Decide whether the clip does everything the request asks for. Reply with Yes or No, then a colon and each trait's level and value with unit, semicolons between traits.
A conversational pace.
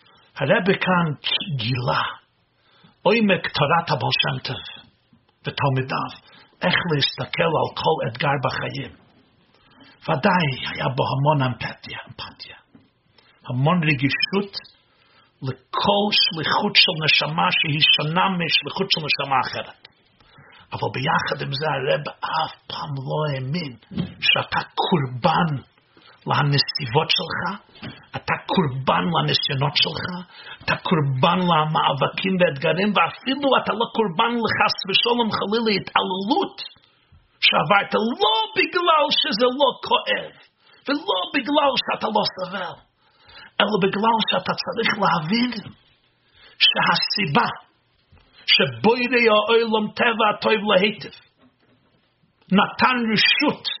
No: slow, 95 wpm